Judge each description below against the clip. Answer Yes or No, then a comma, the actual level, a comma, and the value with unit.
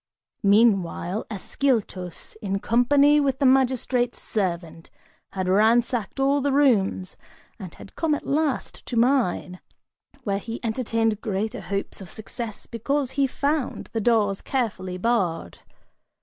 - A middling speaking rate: No, slow, 125 wpm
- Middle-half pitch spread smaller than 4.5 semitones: No, average, 5.2 semitones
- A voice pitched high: Yes, high, 225 Hz